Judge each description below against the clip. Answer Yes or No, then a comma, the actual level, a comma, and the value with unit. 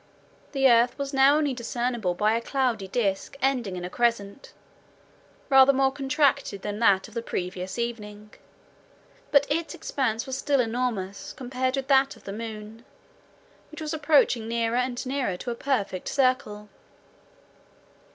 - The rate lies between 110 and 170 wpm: Yes, average, 150 wpm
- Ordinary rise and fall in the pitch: Yes, average, 4.2 semitones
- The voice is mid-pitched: No, high, 245 Hz